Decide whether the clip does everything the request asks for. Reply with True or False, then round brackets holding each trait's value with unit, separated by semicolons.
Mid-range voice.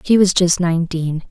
True (175 Hz)